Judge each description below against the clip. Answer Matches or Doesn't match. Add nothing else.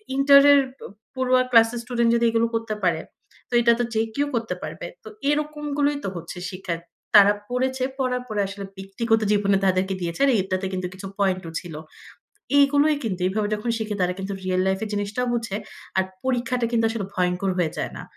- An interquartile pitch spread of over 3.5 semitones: Matches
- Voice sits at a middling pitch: Doesn't match